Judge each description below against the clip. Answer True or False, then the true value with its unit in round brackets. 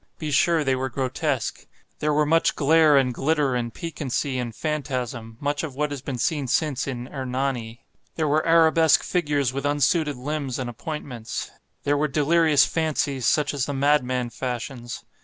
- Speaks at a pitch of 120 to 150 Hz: True (140 Hz)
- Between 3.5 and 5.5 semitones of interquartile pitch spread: False (3.1 semitones)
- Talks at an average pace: True (160 wpm)